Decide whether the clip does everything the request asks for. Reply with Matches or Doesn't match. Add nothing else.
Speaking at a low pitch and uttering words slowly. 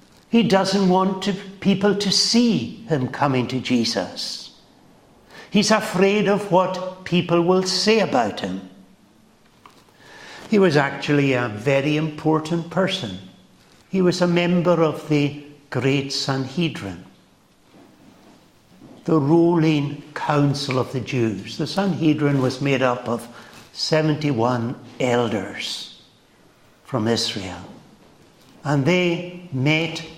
Doesn't match